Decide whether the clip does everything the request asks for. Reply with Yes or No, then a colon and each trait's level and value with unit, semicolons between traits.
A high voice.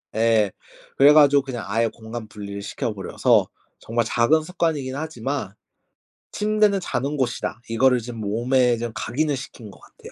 No: low, 120 Hz